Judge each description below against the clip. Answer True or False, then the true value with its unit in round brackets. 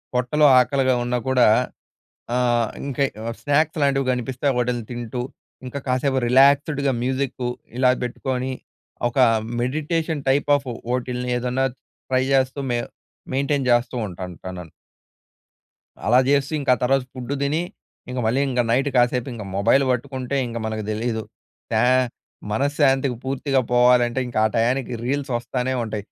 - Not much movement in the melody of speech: True (2.2 semitones)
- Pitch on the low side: True (130 Hz)